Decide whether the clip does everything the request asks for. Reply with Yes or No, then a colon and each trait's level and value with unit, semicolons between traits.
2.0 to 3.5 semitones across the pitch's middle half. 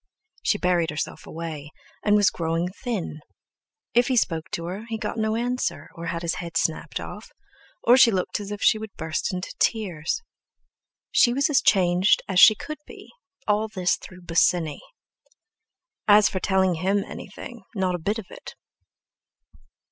No: average, 4.5 semitones